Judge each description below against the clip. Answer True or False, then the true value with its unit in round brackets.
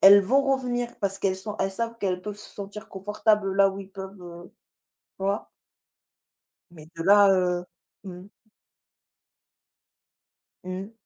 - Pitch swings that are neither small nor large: False (2.0 semitones)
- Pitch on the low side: False (195 Hz)